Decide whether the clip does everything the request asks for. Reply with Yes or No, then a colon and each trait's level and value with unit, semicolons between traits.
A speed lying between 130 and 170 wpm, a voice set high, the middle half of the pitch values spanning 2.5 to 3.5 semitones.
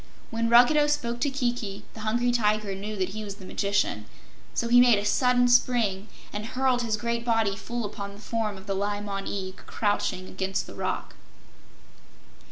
No: average, 180 wpm; high, 215 Hz; average, 3.2 semitones